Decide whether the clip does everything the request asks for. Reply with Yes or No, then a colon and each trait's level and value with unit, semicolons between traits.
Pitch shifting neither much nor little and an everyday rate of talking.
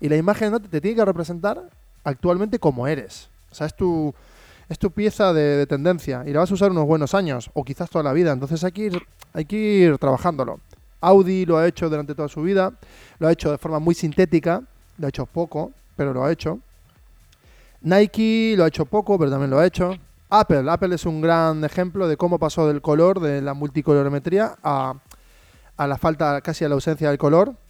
No: average, 3.9 semitones; fast, 215 wpm